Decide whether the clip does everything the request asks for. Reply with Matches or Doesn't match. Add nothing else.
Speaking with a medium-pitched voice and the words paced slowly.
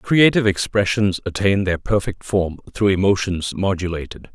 Doesn't match